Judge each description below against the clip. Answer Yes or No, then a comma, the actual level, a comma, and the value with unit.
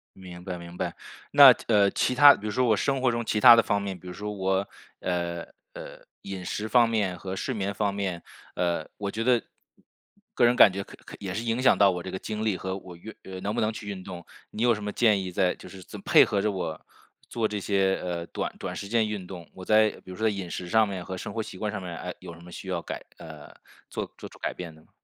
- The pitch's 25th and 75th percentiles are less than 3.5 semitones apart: Yes, average, 3.1 semitones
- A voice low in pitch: Yes, low, 100 Hz